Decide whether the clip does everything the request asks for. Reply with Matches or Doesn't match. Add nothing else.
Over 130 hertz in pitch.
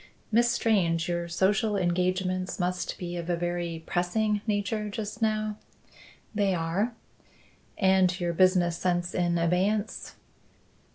Matches